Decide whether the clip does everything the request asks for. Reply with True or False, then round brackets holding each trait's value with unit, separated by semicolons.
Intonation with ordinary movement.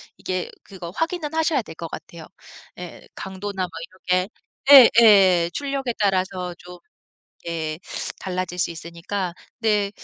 True (3.1 semitones)